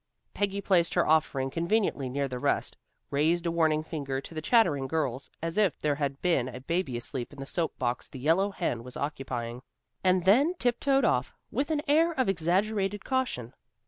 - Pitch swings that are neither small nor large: No, wide, 6.7 semitones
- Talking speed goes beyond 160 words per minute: Yes, average, 185 wpm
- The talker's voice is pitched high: No, medium, 160 Hz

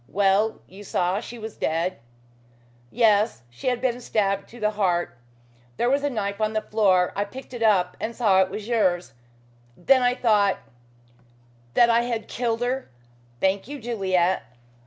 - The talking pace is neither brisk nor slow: Yes, average, 170 wpm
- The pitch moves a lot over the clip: No, average, 4.0 semitones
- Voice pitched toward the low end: No, high, 210 Hz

